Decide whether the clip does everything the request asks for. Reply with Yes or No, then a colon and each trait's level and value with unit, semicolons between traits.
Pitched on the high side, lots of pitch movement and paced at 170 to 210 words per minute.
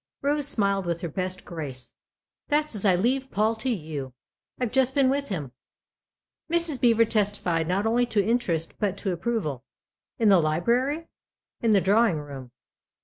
Yes: high, 205 Hz; wide, 6.3 semitones; average, 180 wpm